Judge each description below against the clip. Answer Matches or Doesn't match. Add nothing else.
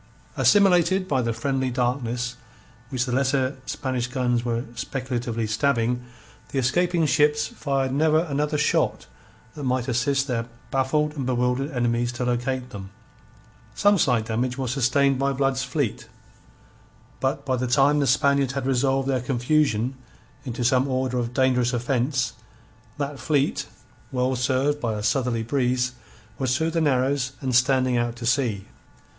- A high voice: Doesn't match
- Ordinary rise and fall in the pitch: Doesn't match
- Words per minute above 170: Doesn't match